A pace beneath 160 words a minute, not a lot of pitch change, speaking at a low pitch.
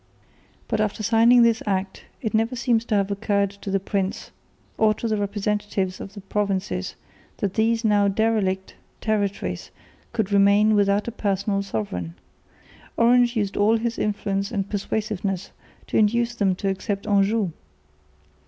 No: average, 145 wpm; narrow, 2.0 semitones; high, 205 Hz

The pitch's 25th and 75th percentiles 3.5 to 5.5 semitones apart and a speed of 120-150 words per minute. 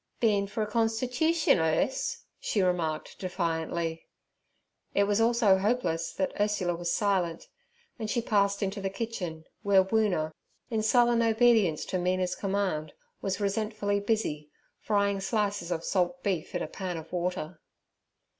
Yes: average, 3.8 semitones; average, 145 wpm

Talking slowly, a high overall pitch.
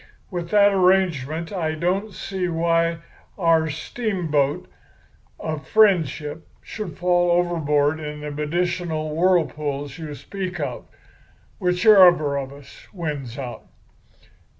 No: slow, 105 wpm; medium, 165 Hz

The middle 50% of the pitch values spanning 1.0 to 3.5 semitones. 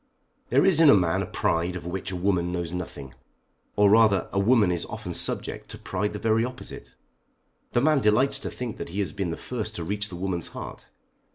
No: average, 4.3 semitones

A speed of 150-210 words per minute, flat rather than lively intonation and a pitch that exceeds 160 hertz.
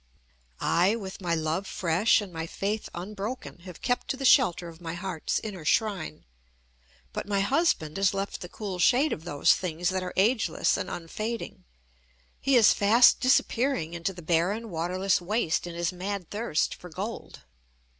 No: average, 165 wpm; average, 4.0 semitones; high, 190 Hz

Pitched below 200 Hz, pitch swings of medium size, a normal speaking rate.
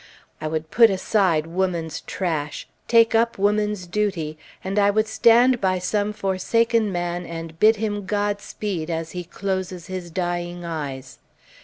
Yes: medium, 185 Hz; average, 3.6 semitones; average, 145 wpm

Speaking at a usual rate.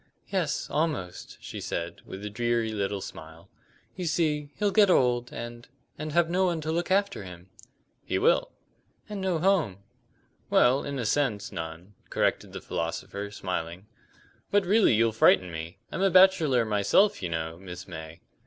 Yes: average, 160 wpm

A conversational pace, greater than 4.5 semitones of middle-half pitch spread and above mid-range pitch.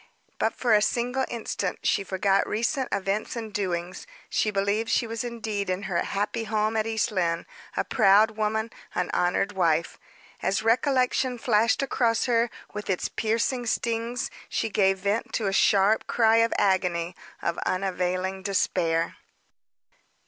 No: average, 150 wpm; average, 3.1 semitones; high, 210 Hz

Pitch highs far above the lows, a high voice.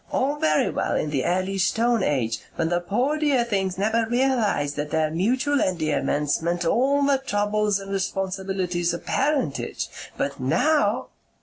Yes: wide, 6.3 semitones; high, 195 Hz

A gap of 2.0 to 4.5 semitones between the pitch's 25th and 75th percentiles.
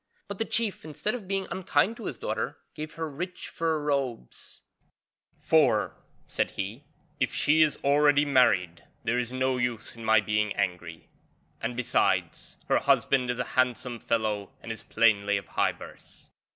No: wide, 5.5 semitones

